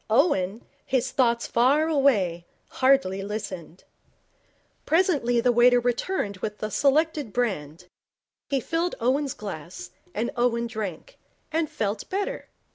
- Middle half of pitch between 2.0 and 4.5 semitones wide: No, wide, 5.4 semitones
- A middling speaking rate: No, slow, 120 wpm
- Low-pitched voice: No, high, 240 Hz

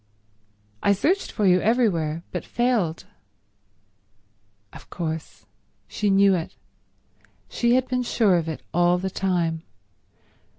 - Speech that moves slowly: Yes, slow, 120 wpm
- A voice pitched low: No, high, 190 Hz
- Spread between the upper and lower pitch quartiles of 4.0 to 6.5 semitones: Yes, average, 5.3 semitones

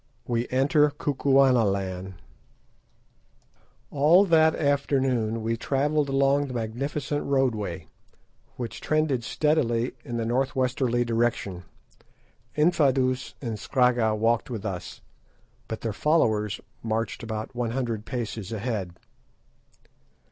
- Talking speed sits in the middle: No, slow, 105 wpm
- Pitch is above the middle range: No, low, 120 Hz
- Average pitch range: Yes, average, 3.8 semitones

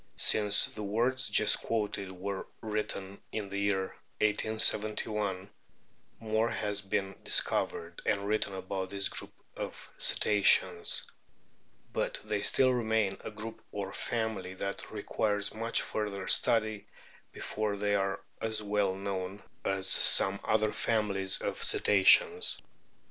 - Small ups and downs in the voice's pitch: Yes, narrow, 1.8 semitones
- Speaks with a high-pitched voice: No, low, 105 Hz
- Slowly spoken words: Yes, slow, 125 wpm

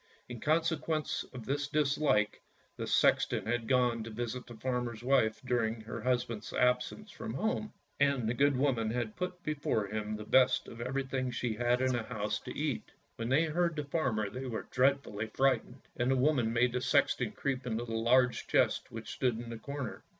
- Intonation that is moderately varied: Yes, average, 3.3 semitones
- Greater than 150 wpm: Yes, average, 190 wpm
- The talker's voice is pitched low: Yes, low, 125 Hz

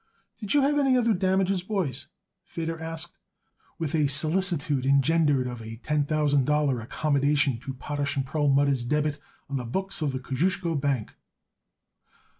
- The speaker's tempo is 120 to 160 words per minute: Yes, average, 150 wpm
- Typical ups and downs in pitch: Yes, average, 3.8 semitones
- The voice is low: No, medium, 150 Hz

